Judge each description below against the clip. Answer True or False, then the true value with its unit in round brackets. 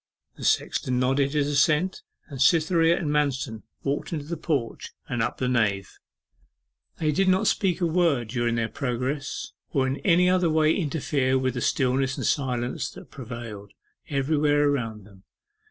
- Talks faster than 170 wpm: False (155 wpm)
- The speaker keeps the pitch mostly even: False (4.0 semitones)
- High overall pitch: False (140 Hz)